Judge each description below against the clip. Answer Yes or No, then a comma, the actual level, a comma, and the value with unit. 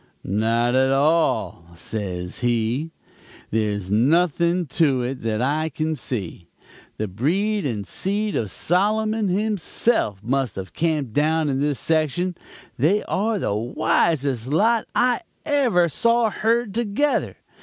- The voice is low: No, medium, 150 Hz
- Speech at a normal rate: No, slow, 125 wpm